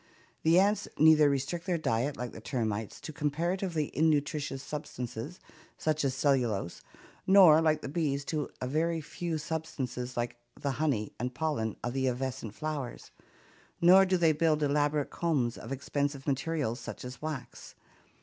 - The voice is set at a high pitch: No, medium, 145 Hz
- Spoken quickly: No, average, 150 wpm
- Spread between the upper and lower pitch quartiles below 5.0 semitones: Yes, average, 3.8 semitones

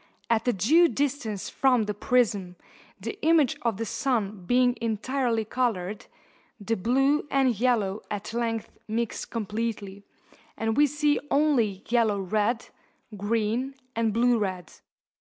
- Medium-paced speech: No, slow, 130 wpm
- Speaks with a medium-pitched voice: No, high, 230 Hz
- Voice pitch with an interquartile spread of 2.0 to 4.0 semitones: Yes, average, 3.4 semitones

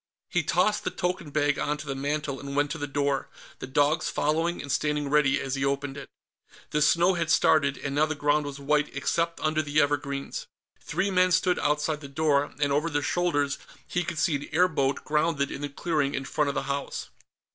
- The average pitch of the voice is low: No, medium, 150 Hz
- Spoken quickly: Yes, fast, 210 wpm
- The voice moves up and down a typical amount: No, narrow, 2.1 semitones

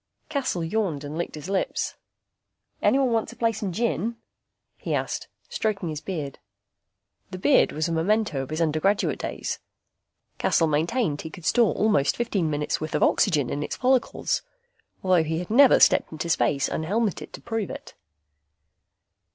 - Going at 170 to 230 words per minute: No, average, 155 wpm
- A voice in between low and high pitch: Yes, medium, 180 Hz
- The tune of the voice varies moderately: No, wide, 6.0 semitones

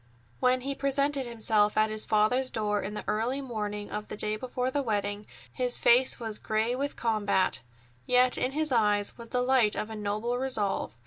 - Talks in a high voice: Yes, high, 230 Hz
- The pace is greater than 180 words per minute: Yes, average, 190 wpm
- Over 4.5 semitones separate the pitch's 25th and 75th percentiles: No, average, 3.3 semitones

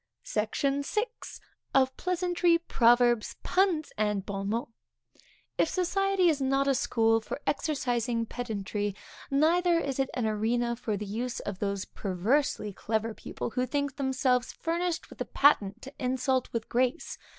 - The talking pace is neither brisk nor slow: Yes, average, 145 wpm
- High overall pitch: Yes, very high, 250 Hz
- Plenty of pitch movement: No, average, 4.7 semitones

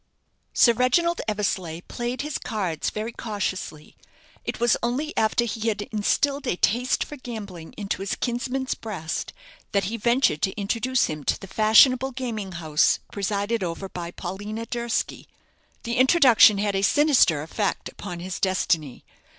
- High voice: Yes, high, 215 Hz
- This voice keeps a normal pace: Yes, average, 150 wpm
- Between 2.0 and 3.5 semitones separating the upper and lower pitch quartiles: No, average, 4.4 semitones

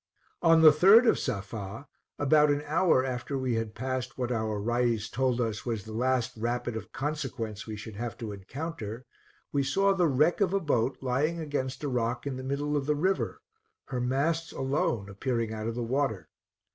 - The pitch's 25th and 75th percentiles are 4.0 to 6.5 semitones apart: Yes, average, 4.4 semitones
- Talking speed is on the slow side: No, average, 190 wpm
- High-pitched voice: No, low, 130 Hz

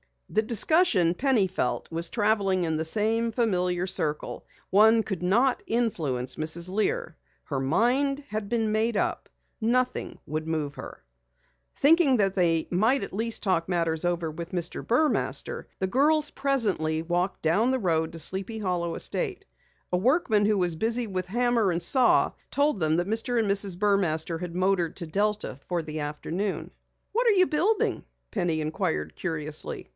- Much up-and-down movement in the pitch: Yes, wide, 5.7 semitones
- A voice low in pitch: No, high, 195 Hz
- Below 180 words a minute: Yes, average, 160 wpm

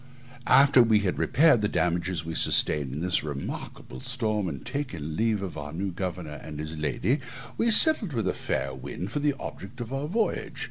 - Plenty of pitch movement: Yes, wide, 8.4 semitones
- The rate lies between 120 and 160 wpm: No, average, 190 wpm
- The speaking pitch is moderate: No, very low, 95 Hz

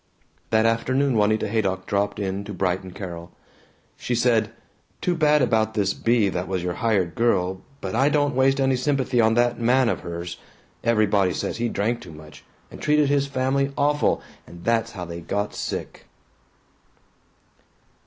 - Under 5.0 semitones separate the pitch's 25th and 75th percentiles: No, wide, 5.5 semitones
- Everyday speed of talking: Yes, average, 165 wpm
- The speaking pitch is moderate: No, low, 110 Hz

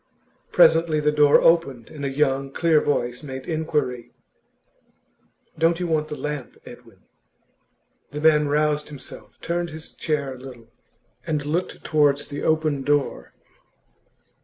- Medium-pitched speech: Yes, medium, 150 Hz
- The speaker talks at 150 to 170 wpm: No, slow, 135 wpm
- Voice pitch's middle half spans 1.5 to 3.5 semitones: Yes, narrow, 2.4 semitones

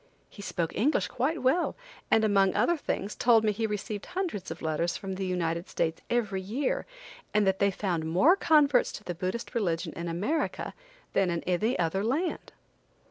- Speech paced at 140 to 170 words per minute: No, average, 180 wpm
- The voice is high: Yes, high, 200 Hz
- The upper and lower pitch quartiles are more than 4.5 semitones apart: Yes, average, 5.3 semitones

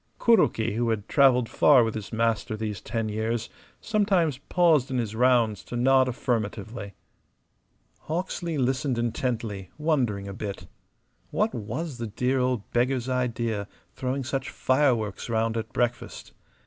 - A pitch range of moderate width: Yes, average, 3.2 semitones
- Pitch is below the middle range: Yes, low, 120 Hz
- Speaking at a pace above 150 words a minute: No, slow, 135 wpm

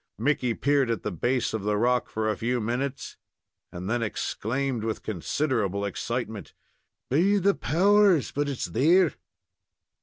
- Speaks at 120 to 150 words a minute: Yes, average, 145 wpm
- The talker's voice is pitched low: Yes, low, 125 Hz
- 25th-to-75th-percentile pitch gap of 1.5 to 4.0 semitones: No, average, 4.8 semitones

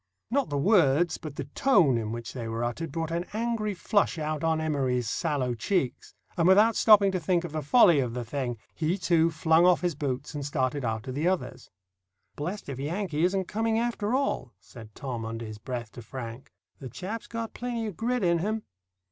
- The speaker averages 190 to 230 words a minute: Yes, average, 200 wpm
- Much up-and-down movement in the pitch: Yes, wide, 7.2 semitones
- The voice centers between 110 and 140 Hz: No, medium, 160 Hz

